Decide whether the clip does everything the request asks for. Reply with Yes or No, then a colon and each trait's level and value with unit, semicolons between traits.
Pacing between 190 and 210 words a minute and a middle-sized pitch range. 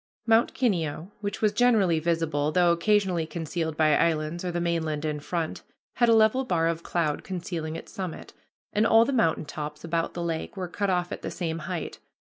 Yes: average, 195 wpm; average, 3.6 semitones